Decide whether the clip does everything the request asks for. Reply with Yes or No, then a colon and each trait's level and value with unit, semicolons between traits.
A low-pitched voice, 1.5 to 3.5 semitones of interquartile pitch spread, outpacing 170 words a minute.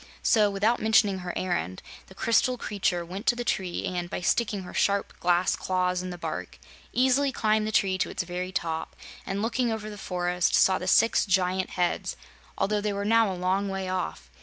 No: high, 190 Hz; average, 2.9 semitones; average, 200 wpm